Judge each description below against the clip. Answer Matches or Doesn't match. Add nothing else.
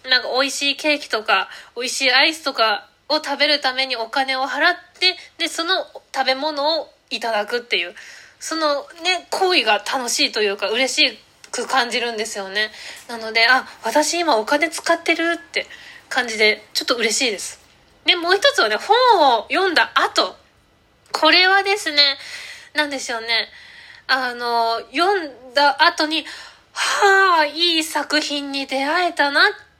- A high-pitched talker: Matches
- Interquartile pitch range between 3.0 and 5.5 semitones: Matches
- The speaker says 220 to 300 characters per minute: Matches